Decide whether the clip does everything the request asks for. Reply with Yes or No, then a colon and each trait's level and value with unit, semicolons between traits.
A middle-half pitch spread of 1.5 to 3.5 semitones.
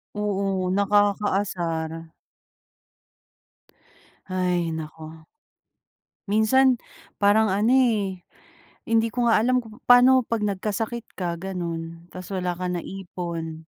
No: average, 3.9 semitones